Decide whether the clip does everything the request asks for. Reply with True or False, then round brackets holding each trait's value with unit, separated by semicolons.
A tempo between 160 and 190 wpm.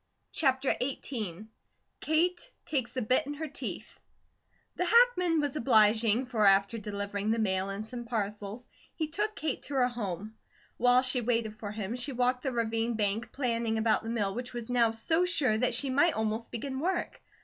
True (180 wpm)